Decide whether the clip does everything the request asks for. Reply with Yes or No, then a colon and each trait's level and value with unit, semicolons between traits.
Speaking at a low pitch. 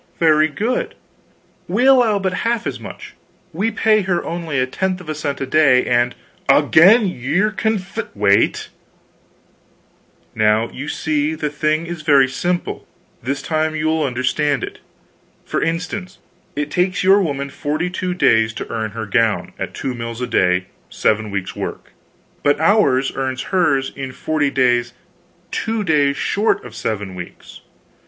No: medium, 150 Hz